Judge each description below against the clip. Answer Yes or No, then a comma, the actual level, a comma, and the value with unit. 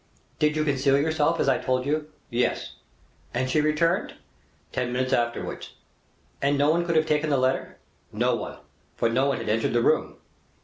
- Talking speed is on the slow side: No, average, 180 wpm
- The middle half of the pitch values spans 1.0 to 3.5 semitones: Yes, average, 3.1 semitones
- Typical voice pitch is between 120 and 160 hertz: Yes, medium, 140 Hz